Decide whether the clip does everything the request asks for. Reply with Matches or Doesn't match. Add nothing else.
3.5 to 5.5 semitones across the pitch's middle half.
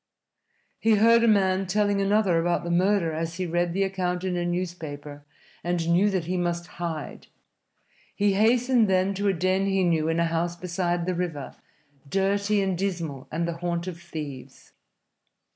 Doesn't match